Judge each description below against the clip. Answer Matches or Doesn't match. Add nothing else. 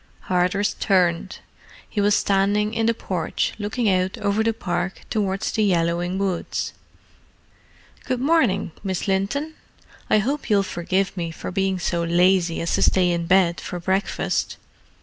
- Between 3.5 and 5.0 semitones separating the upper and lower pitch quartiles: Doesn't match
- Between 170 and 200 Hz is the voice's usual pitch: Matches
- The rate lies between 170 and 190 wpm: Doesn't match